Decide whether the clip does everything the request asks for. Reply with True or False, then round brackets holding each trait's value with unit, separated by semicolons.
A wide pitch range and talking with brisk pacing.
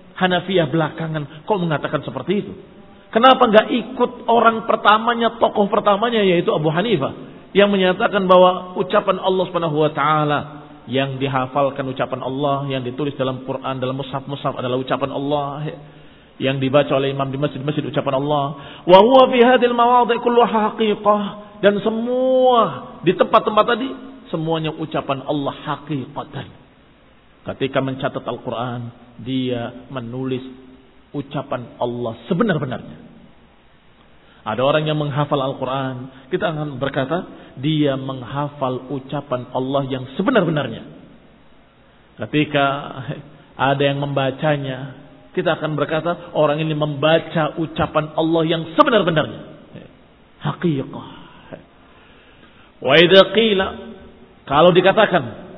False (5.8 semitones; 105 wpm)